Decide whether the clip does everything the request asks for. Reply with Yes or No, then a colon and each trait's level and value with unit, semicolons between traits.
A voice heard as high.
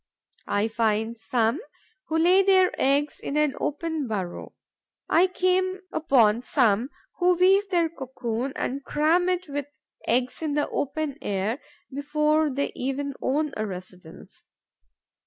Yes: very high, 285 Hz